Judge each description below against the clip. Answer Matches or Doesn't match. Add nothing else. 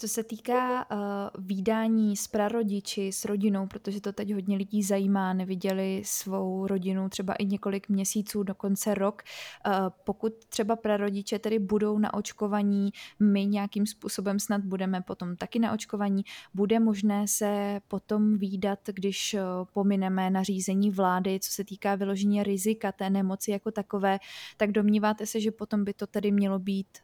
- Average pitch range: Doesn't match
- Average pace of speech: Matches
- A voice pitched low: Doesn't match